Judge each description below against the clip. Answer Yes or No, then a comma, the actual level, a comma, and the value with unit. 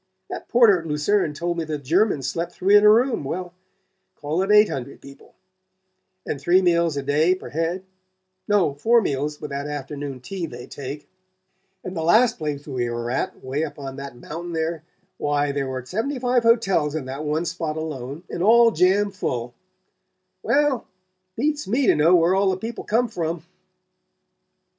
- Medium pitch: Yes, medium, 165 Hz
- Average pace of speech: Yes, average, 180 wpm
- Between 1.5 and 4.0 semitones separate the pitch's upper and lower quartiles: No, wide, 5.6 semitones